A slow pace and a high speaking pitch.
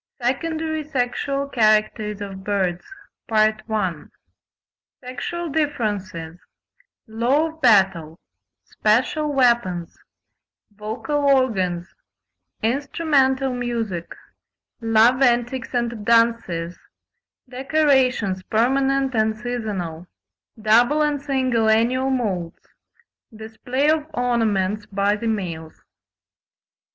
Yes: slow, 60 wpm; high, 230 Hz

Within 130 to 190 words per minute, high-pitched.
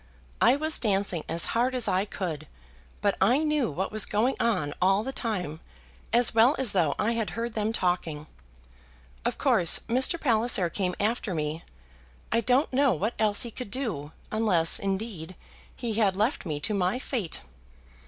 Yes: average, 170 wpm; high, 210 Hz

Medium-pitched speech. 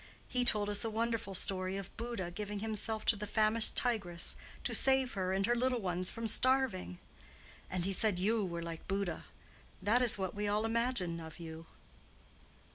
No: high, 205 Hz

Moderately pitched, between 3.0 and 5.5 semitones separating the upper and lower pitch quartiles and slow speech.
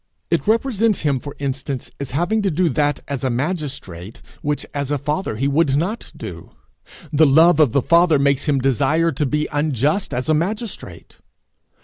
No: medium, 145 Hz; average, 3.6 semitones; average, 175 wpm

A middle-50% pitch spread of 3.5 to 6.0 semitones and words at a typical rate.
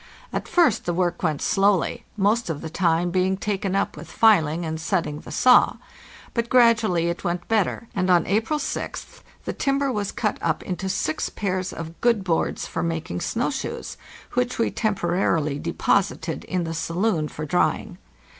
Yes: average, 4.6 semitones; average, 175 wpm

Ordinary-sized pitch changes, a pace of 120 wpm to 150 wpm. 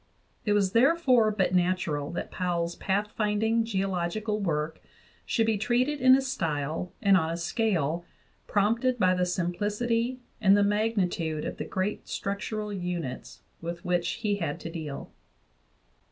Yes: average, 4.3 semitones; average, 140 wpm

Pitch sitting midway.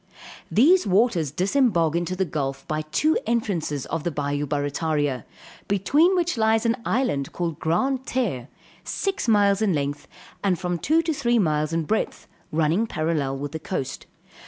Yes: medium, 175 Hz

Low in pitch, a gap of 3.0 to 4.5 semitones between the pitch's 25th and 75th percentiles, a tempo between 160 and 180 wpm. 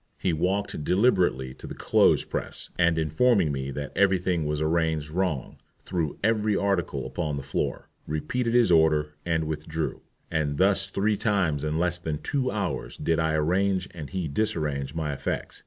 Yes: very low, 80 Hz; average, 4.1 semitones; average, 170 wpm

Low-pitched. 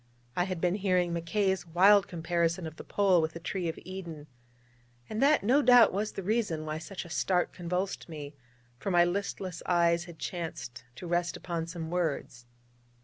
No: medium, 175 Hz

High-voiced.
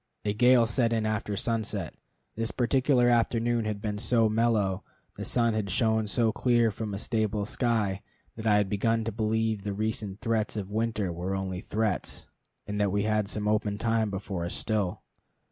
No: low, 110 Hz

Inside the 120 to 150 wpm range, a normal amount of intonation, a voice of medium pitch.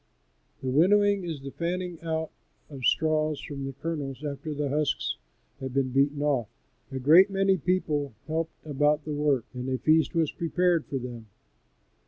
No: average, 170 wpm; average, 3.3 semitones; medium, 150 Hz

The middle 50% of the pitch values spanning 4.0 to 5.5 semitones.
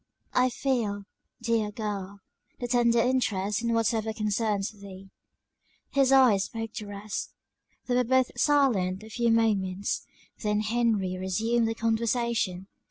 No: average, 2.8 semitones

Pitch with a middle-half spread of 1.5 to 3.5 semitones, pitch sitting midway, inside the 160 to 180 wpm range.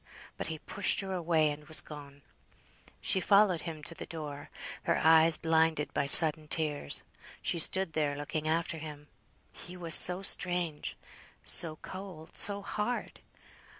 No: average, 2.8 semitones; medium, 160 Hz; average, 150 wpm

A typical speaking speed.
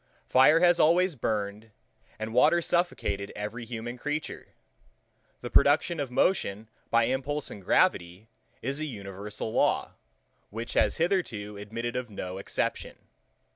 No: slow, 130 wpm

